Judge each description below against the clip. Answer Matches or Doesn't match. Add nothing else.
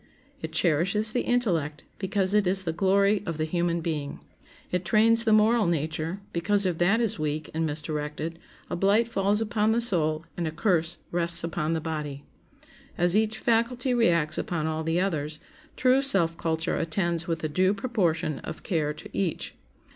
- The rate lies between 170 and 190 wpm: Matches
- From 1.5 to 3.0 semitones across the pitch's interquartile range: Doesn't match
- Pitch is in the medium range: Matches